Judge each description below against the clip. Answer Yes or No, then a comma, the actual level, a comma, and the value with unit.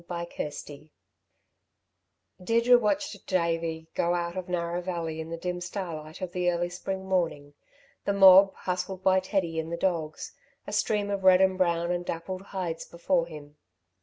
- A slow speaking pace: No, average, 165 wpm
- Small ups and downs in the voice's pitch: Yes, narrow, 2.2 semitones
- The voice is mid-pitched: Yes, medium, 175 Hz